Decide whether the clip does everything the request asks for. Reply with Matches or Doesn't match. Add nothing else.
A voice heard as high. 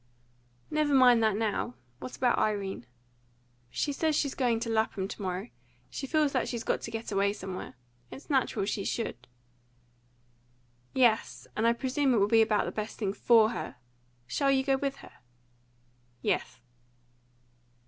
Matches